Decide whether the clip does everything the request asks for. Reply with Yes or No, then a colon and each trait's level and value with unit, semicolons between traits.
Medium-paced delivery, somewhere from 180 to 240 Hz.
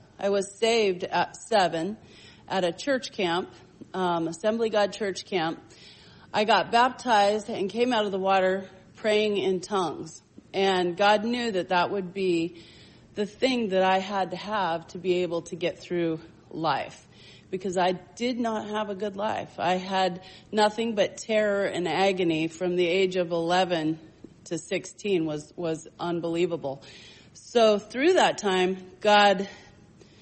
Yes: average, 155 wpm; high, 190 Hz